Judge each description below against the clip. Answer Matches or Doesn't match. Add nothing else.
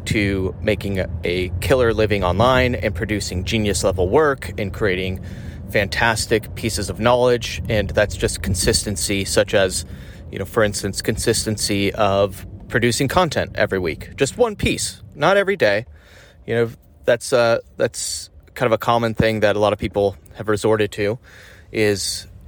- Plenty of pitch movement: Doesn't match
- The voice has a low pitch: Matches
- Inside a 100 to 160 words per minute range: Matches